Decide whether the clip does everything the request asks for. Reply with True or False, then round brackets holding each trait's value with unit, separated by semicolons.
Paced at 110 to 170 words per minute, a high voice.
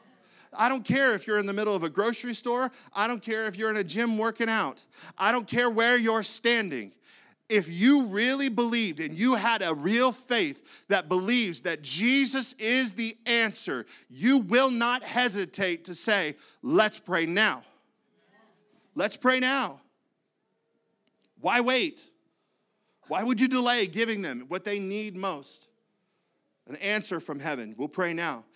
True (160 wpm; 225 Hz)